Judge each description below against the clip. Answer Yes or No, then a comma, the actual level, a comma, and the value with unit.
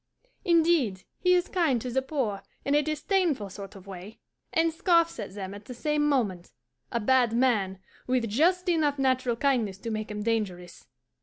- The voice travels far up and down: Yes, wide, 6.8 semitones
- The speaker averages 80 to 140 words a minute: No, average, 200 wpm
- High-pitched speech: Yes, very high, 255 Hz